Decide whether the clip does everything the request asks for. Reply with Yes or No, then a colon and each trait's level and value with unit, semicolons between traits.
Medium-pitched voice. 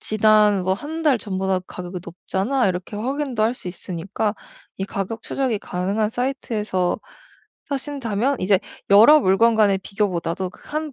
No: high, 210 Hz